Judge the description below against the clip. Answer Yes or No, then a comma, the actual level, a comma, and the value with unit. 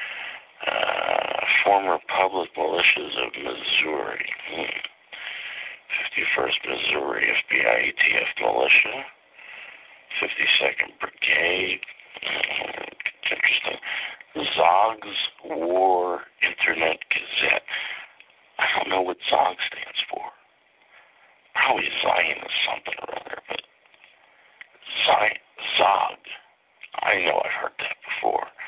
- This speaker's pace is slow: Yes, slow, 85 wpm